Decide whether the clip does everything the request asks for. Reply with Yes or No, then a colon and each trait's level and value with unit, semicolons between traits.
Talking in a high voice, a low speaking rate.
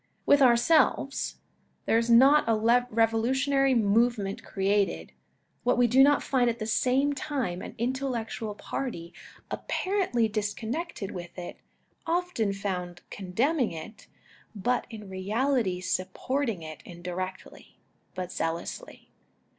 Yes: high, 230 Hz; slow, 115 wpm